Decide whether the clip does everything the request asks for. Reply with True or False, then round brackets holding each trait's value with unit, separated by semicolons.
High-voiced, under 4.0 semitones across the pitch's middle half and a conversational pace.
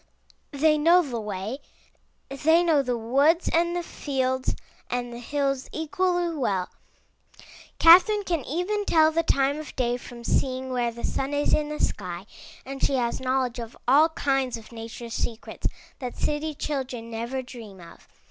False (270 Hz; 4.6 semitones; 160 wpm)